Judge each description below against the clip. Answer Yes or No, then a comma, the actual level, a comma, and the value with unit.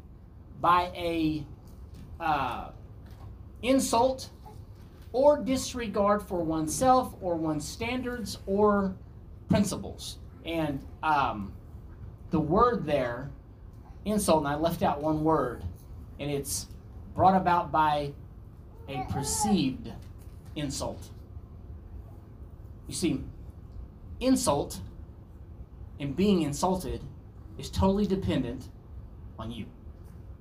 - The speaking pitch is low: Yes, low, 110 Hz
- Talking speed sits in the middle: No, slow, 85 wpm